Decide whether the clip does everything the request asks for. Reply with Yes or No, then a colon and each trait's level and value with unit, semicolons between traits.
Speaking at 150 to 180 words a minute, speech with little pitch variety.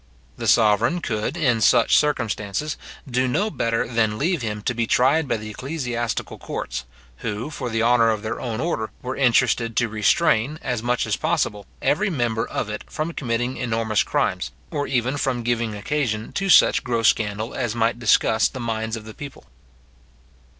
No: average, 175 wpm; average, 3.1 semitones